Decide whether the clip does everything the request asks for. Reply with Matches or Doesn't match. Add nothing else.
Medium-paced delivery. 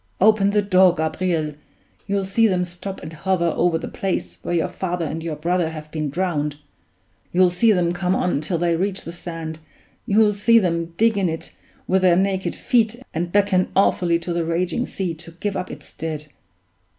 Matches